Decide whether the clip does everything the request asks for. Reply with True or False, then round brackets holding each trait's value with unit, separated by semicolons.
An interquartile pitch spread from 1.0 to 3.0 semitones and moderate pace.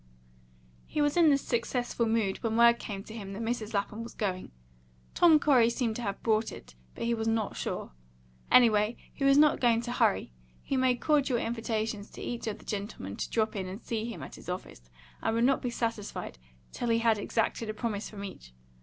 False (2.6 semitones; 210 wpm)